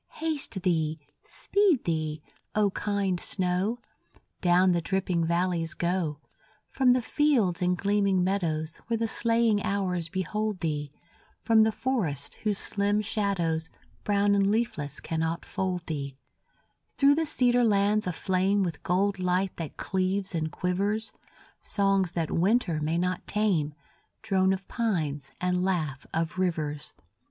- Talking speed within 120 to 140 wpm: Yes, slow, 135 wpm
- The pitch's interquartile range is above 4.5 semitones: No, average, 3.8 semitones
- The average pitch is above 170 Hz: Yes, medium, 185 Hz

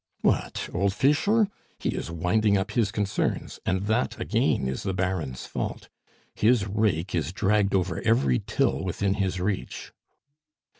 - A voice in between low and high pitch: No, very low, 95 Hz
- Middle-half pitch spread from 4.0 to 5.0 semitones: No, average, 3.1 semitones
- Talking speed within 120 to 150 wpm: Yes, average, 145 wpm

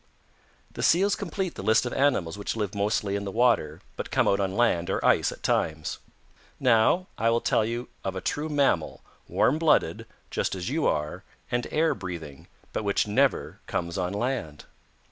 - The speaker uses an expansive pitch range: Yes, wide, 6.3 semitones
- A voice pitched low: Yes, low, 110 Hz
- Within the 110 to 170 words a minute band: No, average, 185 wpm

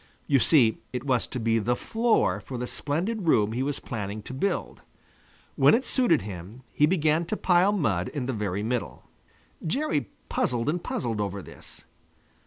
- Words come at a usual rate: Yes, average, 175 wpm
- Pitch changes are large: Yes, wide, 7.0 semitones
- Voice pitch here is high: No, low, 130 Hz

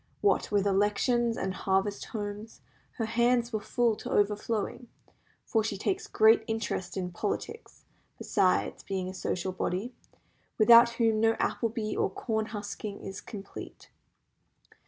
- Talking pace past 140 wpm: No, slow, 135 wpm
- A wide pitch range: No, average, 2.7 semitones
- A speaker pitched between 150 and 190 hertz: No, high, 215 Hz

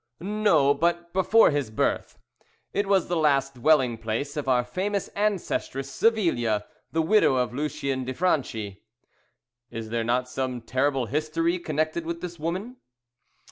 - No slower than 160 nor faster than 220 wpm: No, average, 140 wpm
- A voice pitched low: No, medium, 150 Hz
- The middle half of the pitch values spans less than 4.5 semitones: No, wide, 5.4 semitones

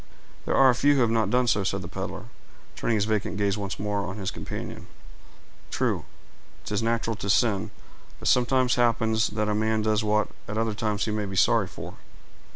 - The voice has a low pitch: Yes, low, 110 Hz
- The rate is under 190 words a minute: No, average, 195 wpm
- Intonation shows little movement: Yes, narrow, 2.0 semitones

